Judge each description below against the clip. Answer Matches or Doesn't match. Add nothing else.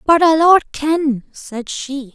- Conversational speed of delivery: Matches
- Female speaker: Matches